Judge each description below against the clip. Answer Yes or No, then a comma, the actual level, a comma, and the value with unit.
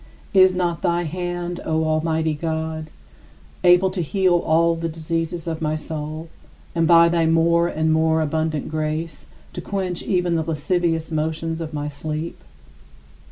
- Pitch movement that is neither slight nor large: No, narrow, 1.6 semitones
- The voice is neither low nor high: Yes, medium, 165 Hz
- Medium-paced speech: Yes, average, 155 wpm